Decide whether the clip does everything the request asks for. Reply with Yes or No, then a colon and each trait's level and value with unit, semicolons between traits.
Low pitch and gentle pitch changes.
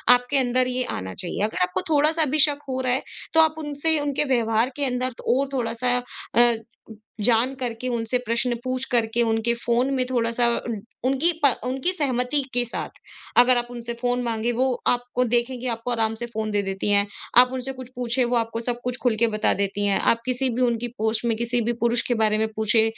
No: high, 245 Hz; narrow, 2.0 semitones